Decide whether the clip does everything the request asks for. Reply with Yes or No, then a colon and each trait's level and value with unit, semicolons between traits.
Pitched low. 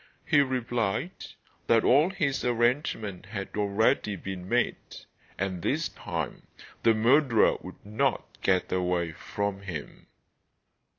Yes: low, 105 Hz